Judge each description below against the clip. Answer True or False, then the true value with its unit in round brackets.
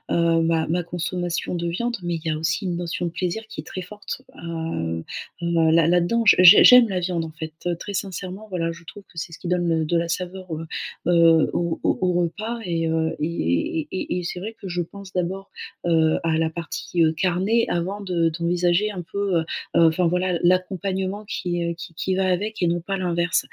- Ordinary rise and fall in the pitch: False (2.1 semitones)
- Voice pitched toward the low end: False (175 Hz)